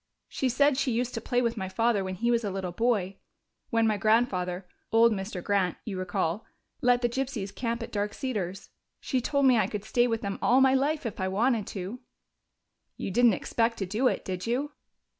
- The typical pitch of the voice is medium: No, high, 225 Hz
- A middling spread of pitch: Yes, average, 4.1 semitones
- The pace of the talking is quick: Yes, fast, 210 wpm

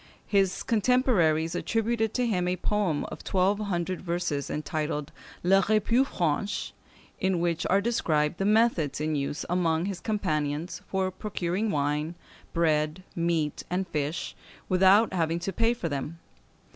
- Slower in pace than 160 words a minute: Yes, average, 140 wpm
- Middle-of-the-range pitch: Yes, medium, 180 Hz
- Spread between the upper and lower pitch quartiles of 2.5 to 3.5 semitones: No, average, 4.3 semitones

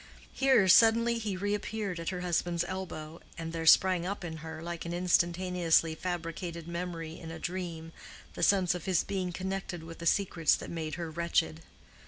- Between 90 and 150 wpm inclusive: No, average, 175 wpm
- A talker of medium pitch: Yes, medium, 175 Hz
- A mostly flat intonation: Yes, narrow, 2.2 semitones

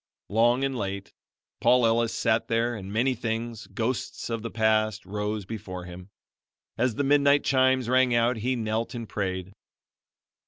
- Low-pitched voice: Yes, low, 115 Hz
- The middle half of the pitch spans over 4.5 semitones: No, average, 2.8 semitones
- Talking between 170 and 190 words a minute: No, average, 155 wpm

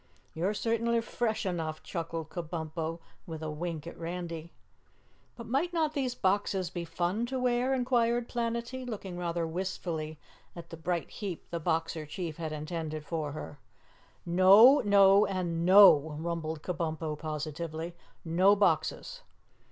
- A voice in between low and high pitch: Yes, medium, 175 Hz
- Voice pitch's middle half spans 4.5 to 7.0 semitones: Yes, average, 4.8 semitones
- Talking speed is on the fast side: No, slow, 135 wpm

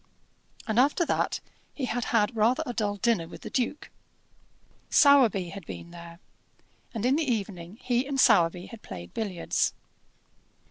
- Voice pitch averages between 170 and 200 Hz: No, high, 220 Hz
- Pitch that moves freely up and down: Yes, wide, 5.8 semitones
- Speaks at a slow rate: No, average, 150 wpm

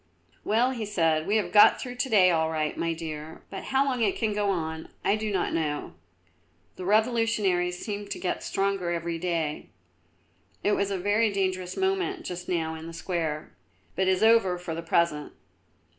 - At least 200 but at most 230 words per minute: No, average, 185 wpm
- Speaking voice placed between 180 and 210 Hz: Yes, medium, 185 Hz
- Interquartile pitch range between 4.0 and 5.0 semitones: Yes, average, 4.3 semitones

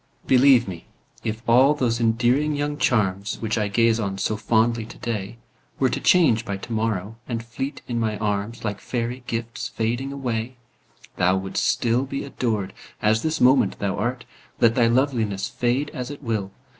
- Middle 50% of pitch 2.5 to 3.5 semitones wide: Yes, average, 2.8 semitones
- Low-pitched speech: Yes, low, 115 Hz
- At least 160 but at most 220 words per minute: Yes, average, 170 wpm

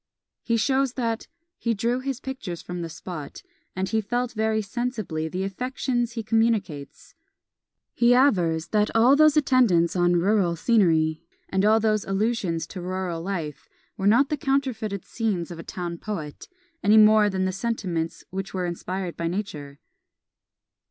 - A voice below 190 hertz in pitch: No, high, 205 Hz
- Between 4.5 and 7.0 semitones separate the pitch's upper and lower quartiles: Yes, average, 5.0 semitones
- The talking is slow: No, average, 155 wpm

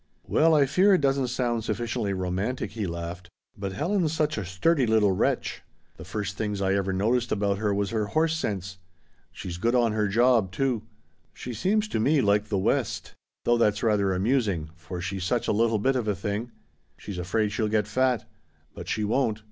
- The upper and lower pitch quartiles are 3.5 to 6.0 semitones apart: Yes, average, 4.1 semitones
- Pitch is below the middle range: Yes, low, 110 Hz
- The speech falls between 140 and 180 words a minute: No, average, 195 wpm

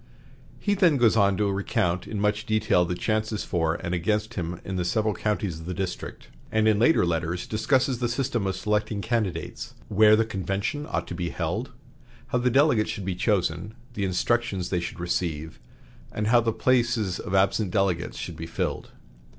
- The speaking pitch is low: Yes, low, 105 Hz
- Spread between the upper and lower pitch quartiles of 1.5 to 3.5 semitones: No, average, 3.9 semitones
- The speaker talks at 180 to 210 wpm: Yes, average, 185 wpm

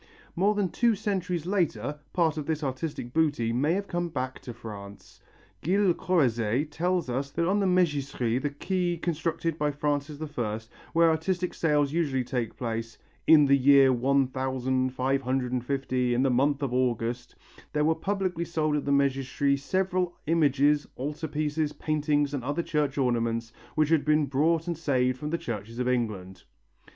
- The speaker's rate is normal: Yes, average, 170 wpm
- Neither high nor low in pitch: Yes, medium, 145 Hz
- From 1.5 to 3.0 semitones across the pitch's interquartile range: No, average, 4.3 semitones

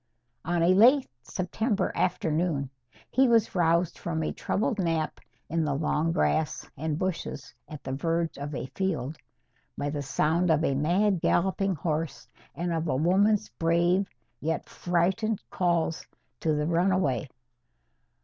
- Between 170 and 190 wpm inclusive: No, average, 140 wpm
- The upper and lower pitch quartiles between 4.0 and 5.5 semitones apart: No, average, 3.3 semitones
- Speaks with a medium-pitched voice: Yes, medium, 170 Hz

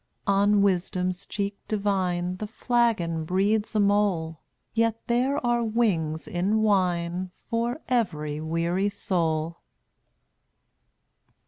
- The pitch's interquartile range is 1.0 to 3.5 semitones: No, average, 4.1 semitones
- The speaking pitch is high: Yes, high, 195 Hz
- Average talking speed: No, slow, 100 wpm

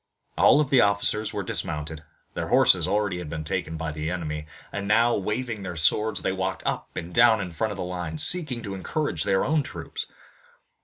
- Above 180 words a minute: Yes, average, 195 wpm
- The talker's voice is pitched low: Yes, very low, 95 Hz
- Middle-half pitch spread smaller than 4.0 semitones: No, average, 5.1 semitones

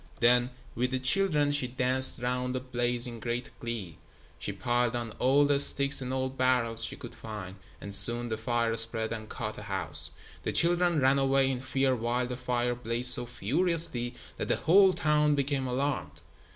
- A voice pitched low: Yes, low, 125 Hz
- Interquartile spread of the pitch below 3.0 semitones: Yes, narrow, 2.5 semitones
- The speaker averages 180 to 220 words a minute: Yes, average, 185 wpm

